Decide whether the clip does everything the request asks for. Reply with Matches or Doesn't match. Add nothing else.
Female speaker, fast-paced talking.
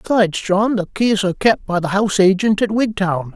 Doesn't match